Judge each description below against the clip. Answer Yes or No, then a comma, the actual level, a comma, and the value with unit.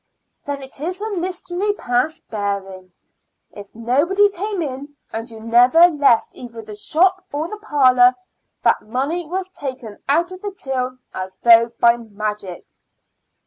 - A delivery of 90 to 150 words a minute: Yes, average, 145 wpm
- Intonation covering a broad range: Yes, wide, 7.4 semitones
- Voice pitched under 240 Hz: No, very high, 265 Hz